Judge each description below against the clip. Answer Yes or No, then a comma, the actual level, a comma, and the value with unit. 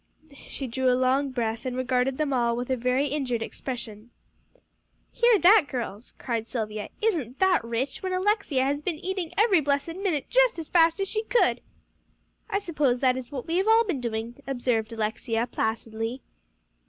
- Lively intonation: Yes, wide, 6.3 semitones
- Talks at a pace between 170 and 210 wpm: Yes, average, 175 wpm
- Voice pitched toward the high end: Yes, very high, 265 Hz